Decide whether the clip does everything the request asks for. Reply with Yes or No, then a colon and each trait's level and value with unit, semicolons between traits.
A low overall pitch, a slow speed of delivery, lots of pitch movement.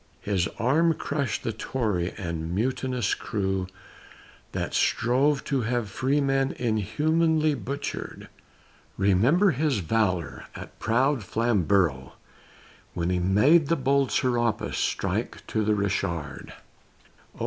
Yes: low, 115 Hz; slow, 110 wpm; wide, 6.2 semitones